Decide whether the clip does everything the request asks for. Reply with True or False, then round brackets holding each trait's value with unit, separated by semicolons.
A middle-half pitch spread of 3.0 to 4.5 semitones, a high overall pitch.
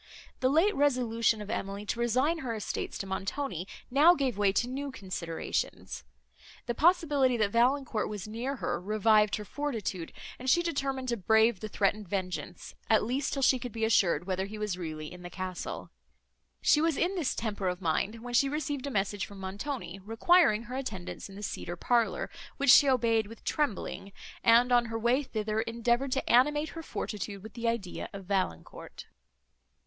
False (5.1 semitones; 230 Hz)